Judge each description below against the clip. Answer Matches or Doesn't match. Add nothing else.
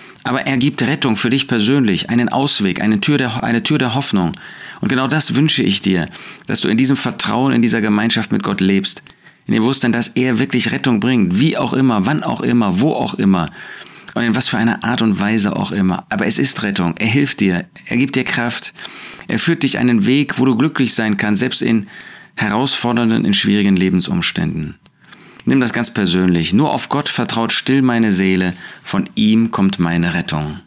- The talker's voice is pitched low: Matches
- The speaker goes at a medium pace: Doesn't match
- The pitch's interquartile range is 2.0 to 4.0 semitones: Doesn't match